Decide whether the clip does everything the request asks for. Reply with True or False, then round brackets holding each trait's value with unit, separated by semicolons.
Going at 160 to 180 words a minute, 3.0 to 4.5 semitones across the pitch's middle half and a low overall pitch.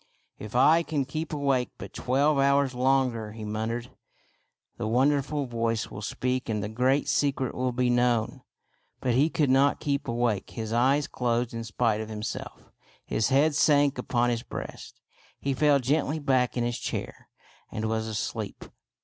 True (170 wpm; 3.3 semitones; 125 Hz)